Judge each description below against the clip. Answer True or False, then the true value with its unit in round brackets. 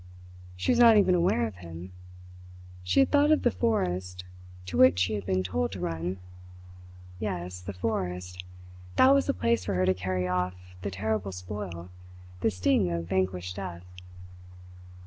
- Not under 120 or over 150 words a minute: False (165 wpm)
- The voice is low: True (90 Hz)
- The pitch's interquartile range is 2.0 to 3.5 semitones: True (2.9 semitones)